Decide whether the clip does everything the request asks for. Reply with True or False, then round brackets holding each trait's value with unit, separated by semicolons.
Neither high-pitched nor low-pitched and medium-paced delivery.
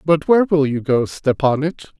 True (150 Hz; 180 wpm)